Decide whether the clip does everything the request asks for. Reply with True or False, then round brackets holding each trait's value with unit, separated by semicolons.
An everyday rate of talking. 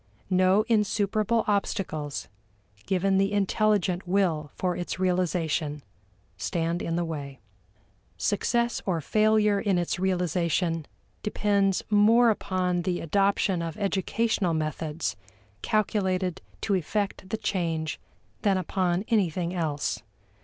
False (110 wpm)